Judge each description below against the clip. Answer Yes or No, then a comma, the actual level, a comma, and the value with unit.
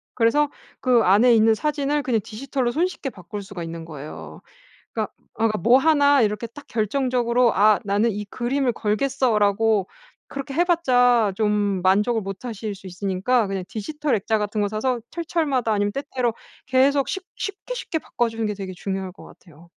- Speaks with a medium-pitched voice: No, high, 225 Hz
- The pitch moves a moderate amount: Yes, average, 4.8 semitones